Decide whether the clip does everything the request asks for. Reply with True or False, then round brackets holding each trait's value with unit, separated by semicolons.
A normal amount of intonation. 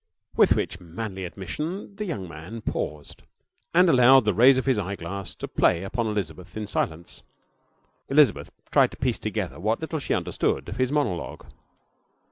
False (6.6 semitones)